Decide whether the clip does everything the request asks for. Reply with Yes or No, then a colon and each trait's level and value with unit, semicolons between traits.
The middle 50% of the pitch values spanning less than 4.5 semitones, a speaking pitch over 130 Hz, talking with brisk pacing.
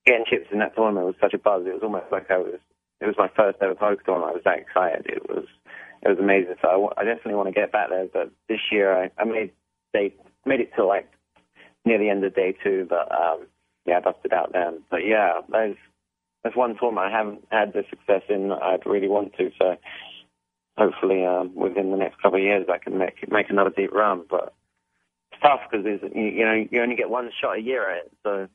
No: average, 2.8 semitones; low, 100 Hz; fast, 240 wpm